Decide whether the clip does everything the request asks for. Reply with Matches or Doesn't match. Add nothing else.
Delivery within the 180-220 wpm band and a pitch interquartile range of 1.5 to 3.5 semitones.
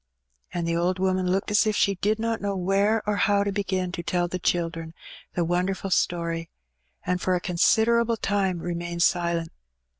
Matches